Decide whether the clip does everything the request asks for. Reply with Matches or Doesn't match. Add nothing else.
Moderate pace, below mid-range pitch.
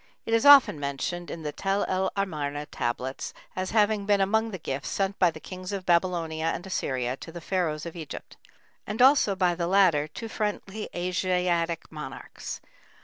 Doesn't match